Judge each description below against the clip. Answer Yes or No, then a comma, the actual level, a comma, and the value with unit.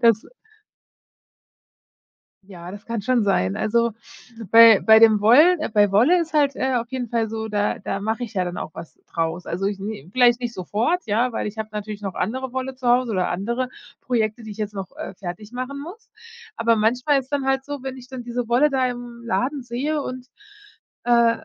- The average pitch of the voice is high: Yes, high, 235 Hz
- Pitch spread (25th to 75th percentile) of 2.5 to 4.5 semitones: Yes, average, 3.6 semitones